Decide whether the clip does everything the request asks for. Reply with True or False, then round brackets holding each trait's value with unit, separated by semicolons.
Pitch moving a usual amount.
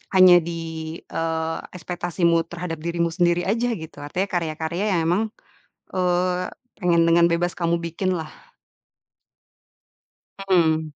False (1.6 semitones)